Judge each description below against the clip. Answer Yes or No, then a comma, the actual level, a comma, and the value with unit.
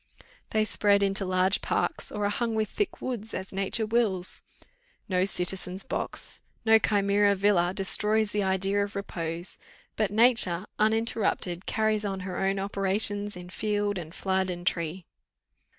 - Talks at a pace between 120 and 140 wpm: No, average, 150 wpm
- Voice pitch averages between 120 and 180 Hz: No, high, 200 Hz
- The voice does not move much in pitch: Yes, narrow, 2.2 semitones